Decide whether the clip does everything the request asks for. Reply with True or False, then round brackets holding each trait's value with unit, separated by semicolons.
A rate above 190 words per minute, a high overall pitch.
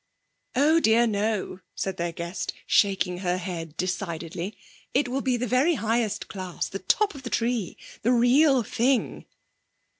False (150 wpm; 220 Hz)